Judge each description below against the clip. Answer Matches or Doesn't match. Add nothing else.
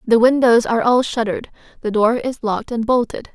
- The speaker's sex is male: Doesn't match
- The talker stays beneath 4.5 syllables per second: Doesn't match